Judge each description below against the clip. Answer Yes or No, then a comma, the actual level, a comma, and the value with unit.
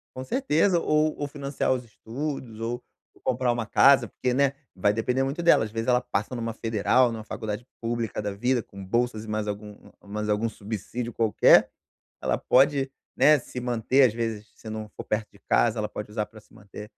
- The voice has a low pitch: Yes, low, 115 Hz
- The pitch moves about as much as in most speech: Yes, average, 3.4 semitones